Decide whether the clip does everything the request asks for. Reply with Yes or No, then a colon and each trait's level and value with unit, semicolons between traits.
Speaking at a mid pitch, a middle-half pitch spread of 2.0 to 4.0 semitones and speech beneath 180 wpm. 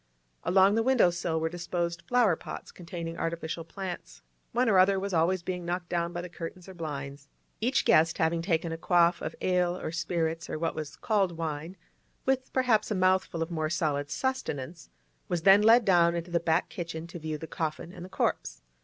No: medium, 170 Hz; narrow, 2.4 semitones; average, 195 wpm